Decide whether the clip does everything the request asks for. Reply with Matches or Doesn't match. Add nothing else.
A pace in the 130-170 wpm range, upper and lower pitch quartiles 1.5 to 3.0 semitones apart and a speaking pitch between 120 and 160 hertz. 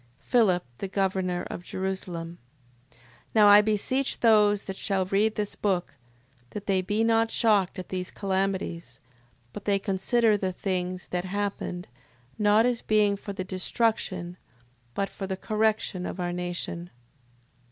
Doesn't match